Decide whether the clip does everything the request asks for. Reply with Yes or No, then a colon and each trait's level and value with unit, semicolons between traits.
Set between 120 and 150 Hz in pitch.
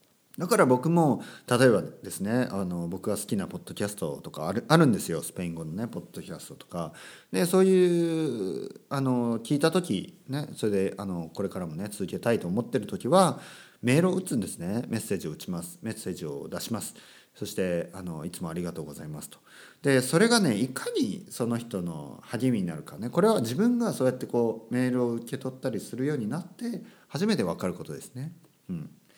Yes: low, 130 Hz